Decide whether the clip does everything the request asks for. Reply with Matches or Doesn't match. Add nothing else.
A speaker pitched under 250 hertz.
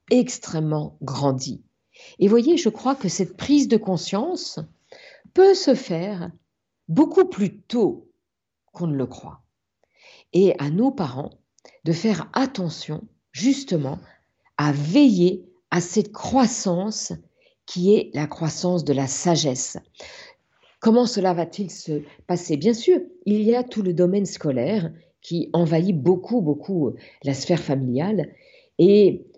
Matches